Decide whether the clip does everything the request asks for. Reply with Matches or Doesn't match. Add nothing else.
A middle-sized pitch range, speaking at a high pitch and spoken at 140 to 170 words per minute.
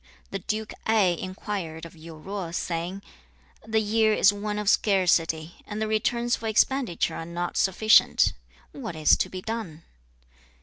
Matches